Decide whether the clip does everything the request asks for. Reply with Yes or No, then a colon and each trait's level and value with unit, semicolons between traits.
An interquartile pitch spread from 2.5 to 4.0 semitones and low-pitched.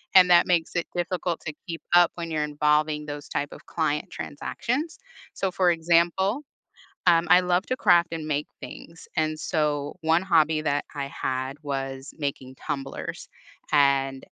No: average, 3.2 semitones; medium, 160 Hz